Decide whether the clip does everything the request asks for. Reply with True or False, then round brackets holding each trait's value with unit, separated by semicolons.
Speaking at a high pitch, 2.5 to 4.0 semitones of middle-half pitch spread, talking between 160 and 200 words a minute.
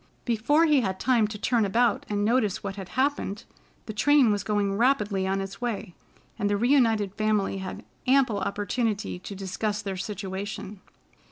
True (210 Hz; 3.2 semitones; 165 wpm)